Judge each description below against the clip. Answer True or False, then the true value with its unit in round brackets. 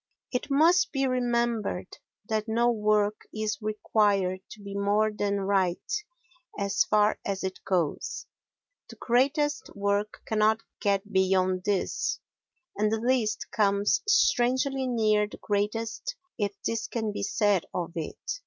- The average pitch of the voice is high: True (210 Hz)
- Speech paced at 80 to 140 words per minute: True (135 wpm)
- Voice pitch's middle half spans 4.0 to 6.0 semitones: False (2.8 semitones)